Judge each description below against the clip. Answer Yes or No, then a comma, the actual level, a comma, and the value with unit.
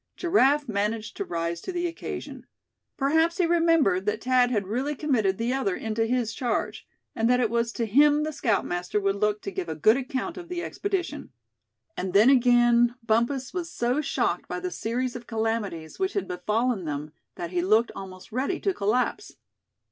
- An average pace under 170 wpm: No, average, 185 wpm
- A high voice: Yes, high, 235 Hz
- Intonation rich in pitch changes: Yes, wide, 5.7 semitones